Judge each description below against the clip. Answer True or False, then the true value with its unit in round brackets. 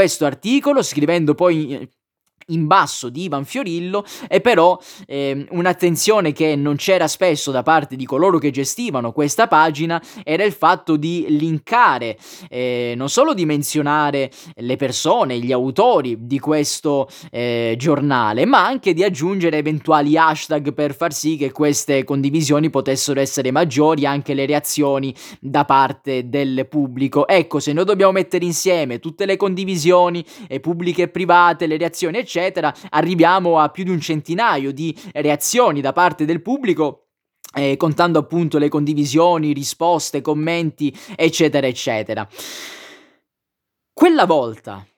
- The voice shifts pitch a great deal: False (3.8 semitones)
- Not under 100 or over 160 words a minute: True (140 wpm)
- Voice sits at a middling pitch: True (155 Hz)